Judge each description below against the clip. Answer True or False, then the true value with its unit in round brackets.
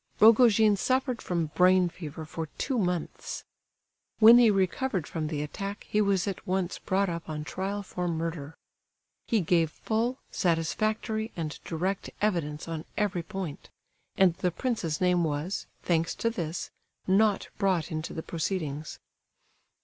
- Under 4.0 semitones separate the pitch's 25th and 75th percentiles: False (4.3 semitones)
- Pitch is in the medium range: True (180 Hz)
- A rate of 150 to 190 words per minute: False (140 wpm)